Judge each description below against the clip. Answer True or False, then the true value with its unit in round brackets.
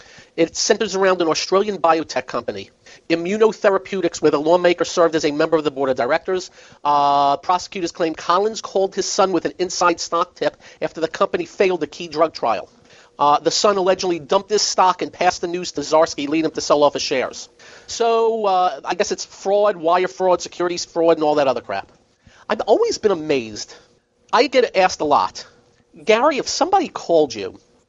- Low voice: False (175 Hz)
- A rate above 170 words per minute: True (190 wpm)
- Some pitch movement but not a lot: True (3.5 semitones)